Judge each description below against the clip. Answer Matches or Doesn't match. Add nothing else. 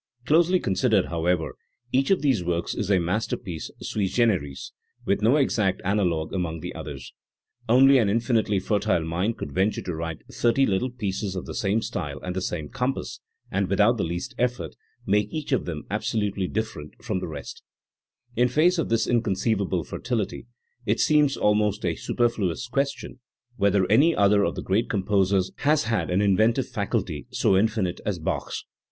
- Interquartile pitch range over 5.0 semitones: Doesn't match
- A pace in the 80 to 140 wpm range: Doesn't match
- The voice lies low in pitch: Matches